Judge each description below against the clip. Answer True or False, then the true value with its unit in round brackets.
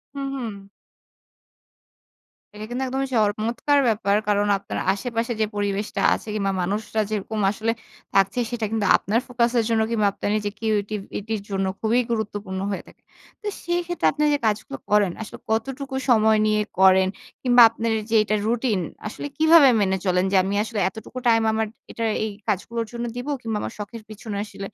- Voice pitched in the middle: False (220 Hz)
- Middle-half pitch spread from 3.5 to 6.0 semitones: False (2.5 semitones)